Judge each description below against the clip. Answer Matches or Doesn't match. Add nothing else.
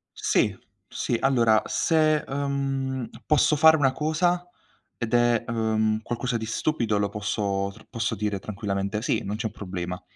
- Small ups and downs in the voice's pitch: Doesn't match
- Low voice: Matches